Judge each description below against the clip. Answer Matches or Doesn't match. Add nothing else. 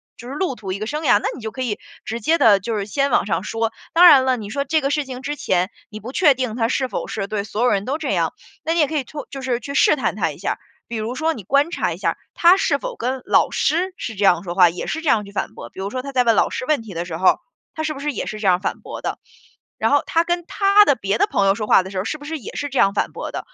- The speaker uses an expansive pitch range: Matches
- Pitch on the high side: Matches